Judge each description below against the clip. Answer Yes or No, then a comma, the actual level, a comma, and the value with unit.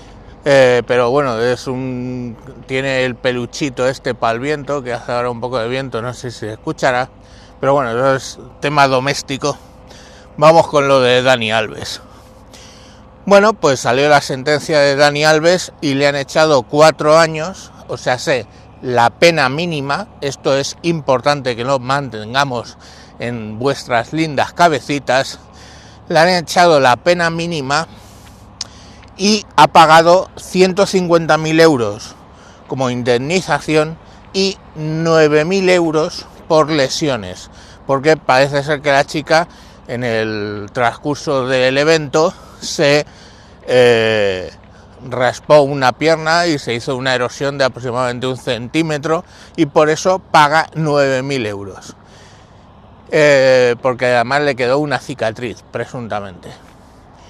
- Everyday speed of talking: No, slow, 130 wpm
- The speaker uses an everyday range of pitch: Yes, average, 4.8 semitones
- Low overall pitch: Yes, low, 130 Hz